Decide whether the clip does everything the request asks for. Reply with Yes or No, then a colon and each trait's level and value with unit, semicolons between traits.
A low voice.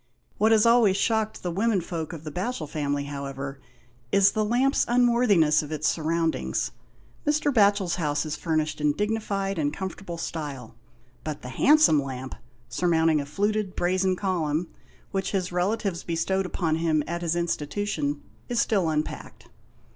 No: medium, 175 Hz